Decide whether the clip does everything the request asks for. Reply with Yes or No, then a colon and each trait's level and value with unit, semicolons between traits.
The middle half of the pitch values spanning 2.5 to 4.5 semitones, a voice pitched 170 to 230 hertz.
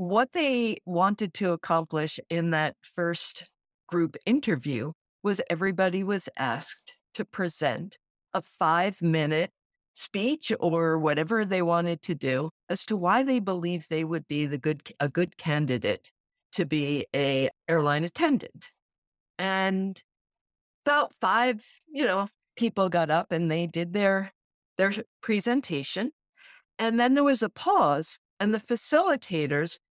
No: average, 5.3 semitones; medium, 185 Hz